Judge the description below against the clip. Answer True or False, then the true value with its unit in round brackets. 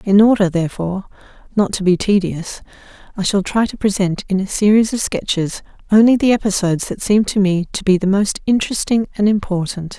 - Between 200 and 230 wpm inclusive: False (185 wpm)